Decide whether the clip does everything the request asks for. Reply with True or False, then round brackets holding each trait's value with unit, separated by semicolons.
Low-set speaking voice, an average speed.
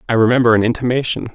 True (120 Hz; 180 wpm)